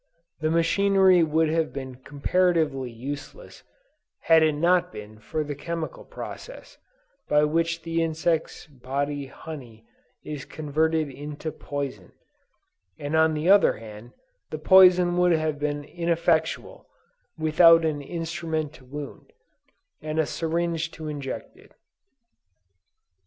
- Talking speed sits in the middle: No, slow, 125 wpm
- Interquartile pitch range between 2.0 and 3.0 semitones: Yes, narrow, 2.6 semitones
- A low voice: No, medium, 155 Hz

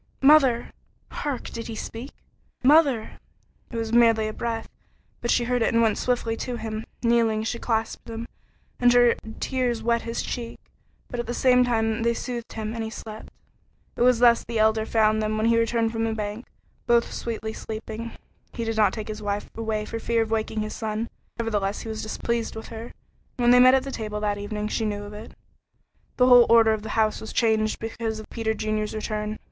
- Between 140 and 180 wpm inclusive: No, average, 200 wpm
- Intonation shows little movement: Yes, narrow, 1.5 semitones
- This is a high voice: Yes, high, 225 Hz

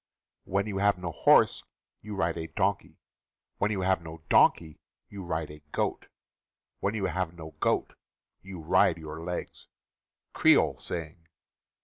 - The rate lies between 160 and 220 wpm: No, average, 150 wpm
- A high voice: No, very low, 85 Hz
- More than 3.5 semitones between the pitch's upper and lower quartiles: No, average, 3.0 semitones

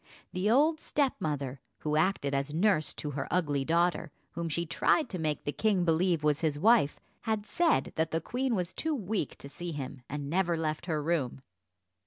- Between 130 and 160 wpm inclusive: No, average, 190 wpm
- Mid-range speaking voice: Yes, medium, 165 Hz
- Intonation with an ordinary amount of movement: Yes, average, 4.8 semitones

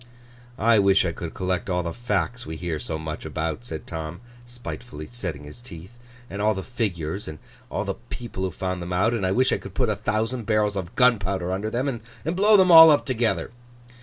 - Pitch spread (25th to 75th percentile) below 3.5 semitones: No, wide, 5.6 semitones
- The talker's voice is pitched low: Yes, low, 100 Hz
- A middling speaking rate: No, fast, 215 wpm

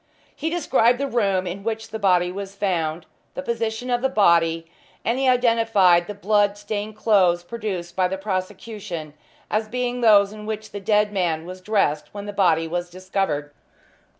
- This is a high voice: Yes, high, 200 Hz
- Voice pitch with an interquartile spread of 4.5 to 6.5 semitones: No, average, 3.7 semitones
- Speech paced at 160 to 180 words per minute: Yes, average, 175 wpm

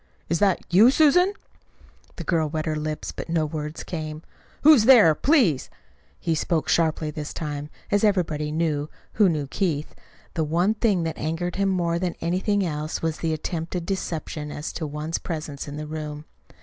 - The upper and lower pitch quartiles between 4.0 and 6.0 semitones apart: No, average, 3.4 semitones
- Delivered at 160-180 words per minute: Yes, average, 175 wpm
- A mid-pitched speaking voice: Yes, medium, 165 Hz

